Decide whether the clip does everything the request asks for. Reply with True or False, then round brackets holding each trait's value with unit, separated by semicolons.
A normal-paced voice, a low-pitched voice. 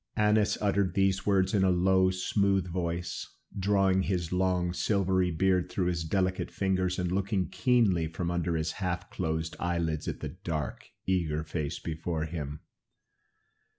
True (150 wpm; 90 Hz)